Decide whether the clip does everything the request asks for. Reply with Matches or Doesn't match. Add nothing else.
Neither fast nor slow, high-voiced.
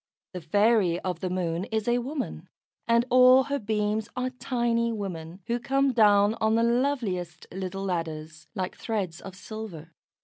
Matches